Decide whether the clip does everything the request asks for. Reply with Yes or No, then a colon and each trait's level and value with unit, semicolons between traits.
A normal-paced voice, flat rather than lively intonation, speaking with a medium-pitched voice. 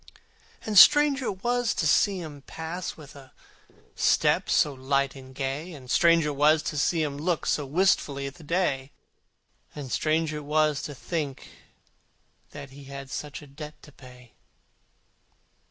No: average, 160 wpm; average, 3.3 semitones; medium, 150 Hz